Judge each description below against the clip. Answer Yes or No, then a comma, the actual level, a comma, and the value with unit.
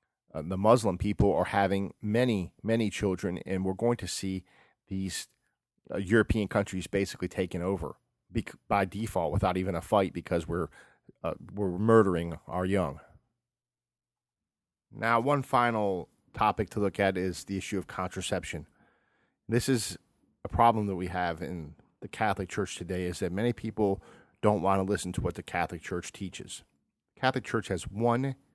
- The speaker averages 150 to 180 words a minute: Yes, average, 160 wpm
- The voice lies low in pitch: Yes, low, 100 Hz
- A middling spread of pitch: Yes, average, 3.1 semitones